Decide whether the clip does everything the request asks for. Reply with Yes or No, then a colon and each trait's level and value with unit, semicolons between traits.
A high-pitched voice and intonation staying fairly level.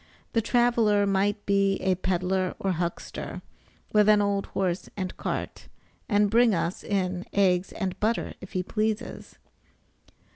Yes: high, 200 Hz; narrow, 2.2 semitones